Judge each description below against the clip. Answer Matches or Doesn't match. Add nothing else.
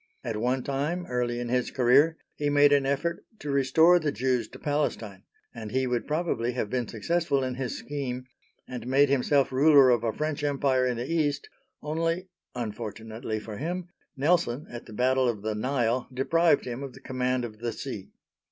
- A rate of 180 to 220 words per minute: Matches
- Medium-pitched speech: Doesn't match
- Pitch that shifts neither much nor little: Matches